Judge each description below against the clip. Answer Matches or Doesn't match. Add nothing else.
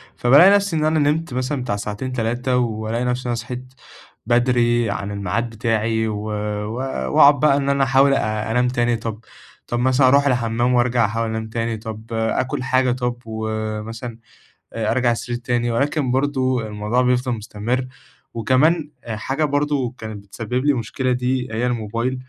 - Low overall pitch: Matches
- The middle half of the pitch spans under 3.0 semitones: Matches